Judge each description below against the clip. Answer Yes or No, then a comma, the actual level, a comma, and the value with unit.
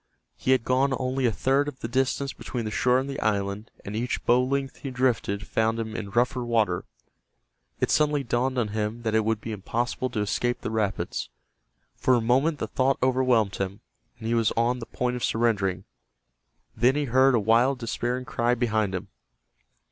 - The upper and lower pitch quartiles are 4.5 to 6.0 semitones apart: No, average, 2.8 semitones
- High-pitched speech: No, low, 120 Hz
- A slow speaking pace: No, average, 195 wpm